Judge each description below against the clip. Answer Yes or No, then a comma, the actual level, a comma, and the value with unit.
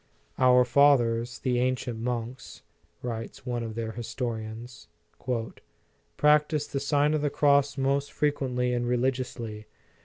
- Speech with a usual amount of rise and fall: Yes, average, 3.1 semitones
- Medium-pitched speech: No, low, 125 Hz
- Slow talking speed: Yes, slow, 125 wpm